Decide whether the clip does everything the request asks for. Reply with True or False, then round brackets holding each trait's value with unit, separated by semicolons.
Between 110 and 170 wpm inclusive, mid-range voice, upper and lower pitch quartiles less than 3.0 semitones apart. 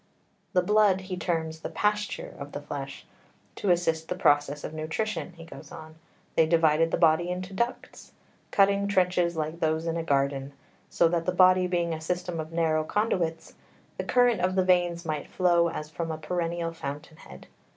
False (180 wpm; 170 Hz; 2.4 semitones)